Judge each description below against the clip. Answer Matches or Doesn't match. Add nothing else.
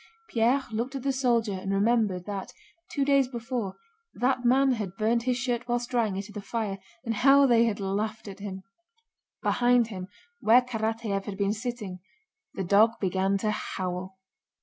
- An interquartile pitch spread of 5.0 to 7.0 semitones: Doesn't match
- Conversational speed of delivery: Matches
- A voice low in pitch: Doesn't match